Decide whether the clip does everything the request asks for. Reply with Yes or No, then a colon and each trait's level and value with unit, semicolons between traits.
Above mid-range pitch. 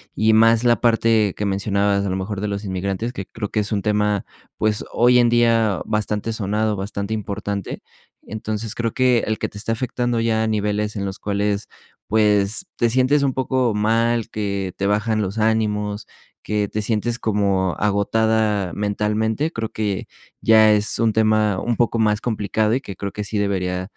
No: low, 105 Hz